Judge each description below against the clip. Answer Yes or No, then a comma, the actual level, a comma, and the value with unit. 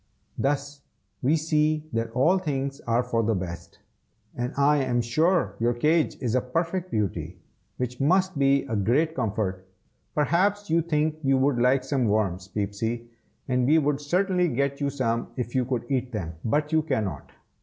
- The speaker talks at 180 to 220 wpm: No, average, 170 wpm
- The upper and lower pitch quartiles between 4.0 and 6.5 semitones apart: Yes, average, 4.9 semitones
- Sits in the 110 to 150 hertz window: Yes, low, 135 Hz